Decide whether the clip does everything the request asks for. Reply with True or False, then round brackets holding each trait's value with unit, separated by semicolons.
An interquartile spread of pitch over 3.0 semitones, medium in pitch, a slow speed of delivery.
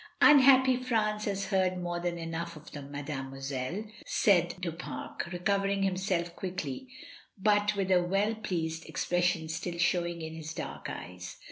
False (3.5 semitones; 175 Hz; 155 wpm)